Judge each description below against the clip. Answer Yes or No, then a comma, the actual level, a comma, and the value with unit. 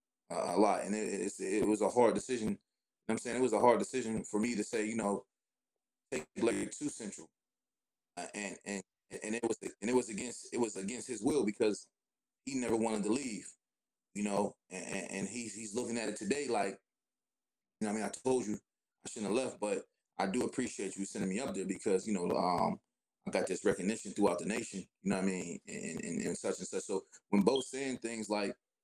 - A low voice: Yes, low, 110 Hz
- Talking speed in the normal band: No, fast, 235 wpm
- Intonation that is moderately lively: Yes, average, 3.1 semitones